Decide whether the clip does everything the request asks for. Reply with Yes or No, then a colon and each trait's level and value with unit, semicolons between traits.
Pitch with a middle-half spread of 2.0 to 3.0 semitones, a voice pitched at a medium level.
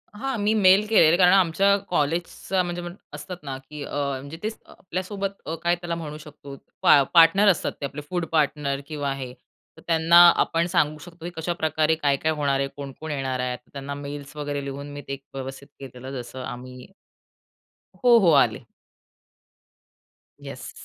No: average, 3.8 semitones; medium, 150 Hz